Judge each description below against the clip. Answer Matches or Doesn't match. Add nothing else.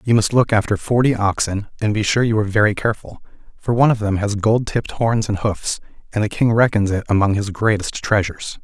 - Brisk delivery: Matches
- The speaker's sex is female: Doesn't match